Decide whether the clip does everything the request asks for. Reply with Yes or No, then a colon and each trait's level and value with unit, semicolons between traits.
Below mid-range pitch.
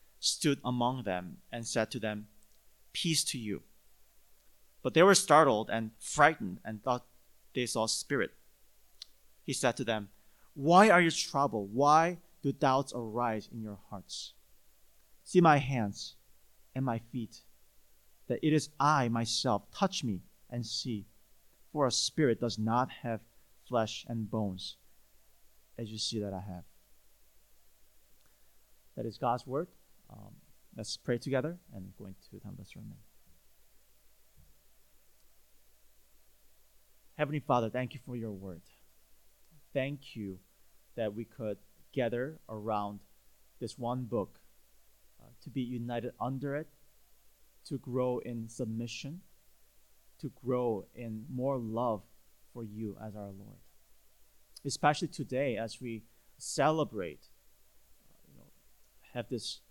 Yes: low, 120 Hz